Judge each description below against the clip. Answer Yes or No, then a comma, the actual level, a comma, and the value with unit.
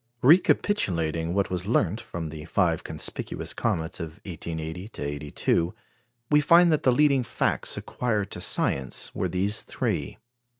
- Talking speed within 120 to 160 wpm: Yes, slow, 135 wpm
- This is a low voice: Yes, very low, 90 Hz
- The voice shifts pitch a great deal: Yes, wide, 7.4 semitones